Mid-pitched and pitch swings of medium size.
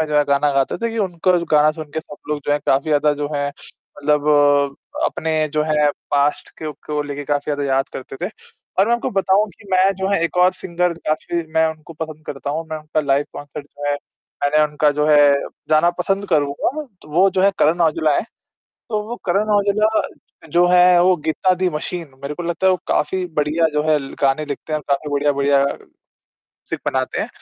Yes: medium, 155 Hz; average, 3.4 semitones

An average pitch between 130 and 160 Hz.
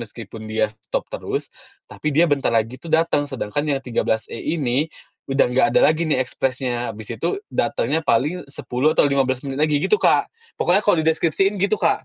Yes: medium, 140 Hz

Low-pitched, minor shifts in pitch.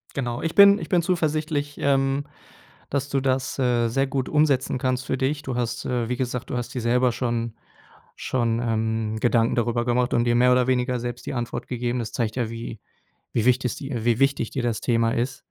Yes: low, 125 Hz; narrow, 2.3 semitones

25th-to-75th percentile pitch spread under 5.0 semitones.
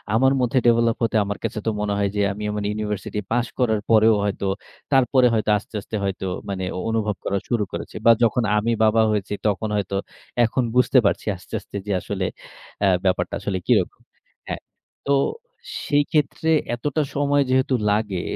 Yes: average, 3.3 semitones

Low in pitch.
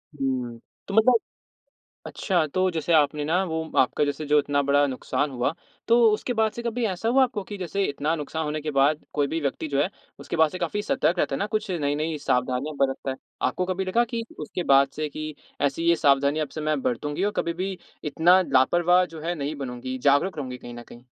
No: medium, 155 Hz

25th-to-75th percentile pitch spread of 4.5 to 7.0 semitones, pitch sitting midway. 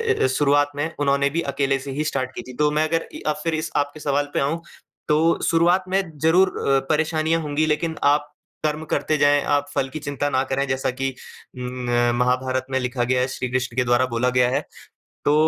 No: average, 3.1 semitones; medium, 145 Hz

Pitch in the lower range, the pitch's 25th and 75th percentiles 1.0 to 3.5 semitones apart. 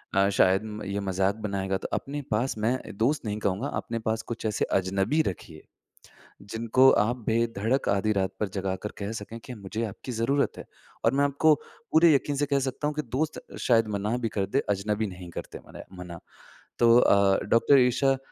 No: low, 110 Hz; average, 4.7 semitones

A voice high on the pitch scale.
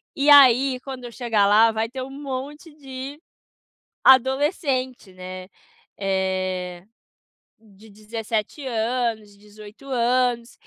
Yes: high, 235 Hz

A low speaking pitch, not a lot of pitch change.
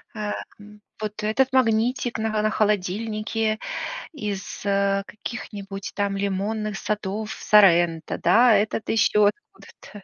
No: high, 210 Hz; narrow, 1.6 semitones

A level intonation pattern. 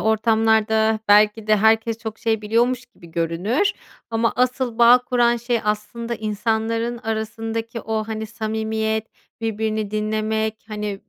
Yes: narrow, 1.1 semitones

